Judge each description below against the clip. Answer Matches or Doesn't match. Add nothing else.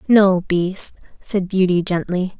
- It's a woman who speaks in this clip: Matches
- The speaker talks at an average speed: Doesn't match